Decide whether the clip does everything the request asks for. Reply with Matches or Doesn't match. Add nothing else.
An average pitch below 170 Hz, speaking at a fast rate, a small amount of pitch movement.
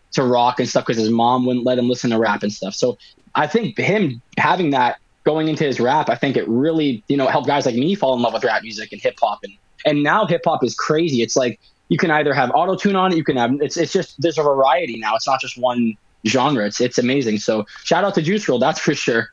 Doesn't match